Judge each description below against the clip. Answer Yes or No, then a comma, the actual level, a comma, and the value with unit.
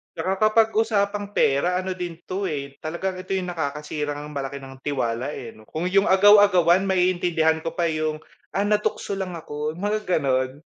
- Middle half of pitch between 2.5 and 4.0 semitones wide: No, average, 4.5 semitones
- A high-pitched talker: No, medium, 175 Hz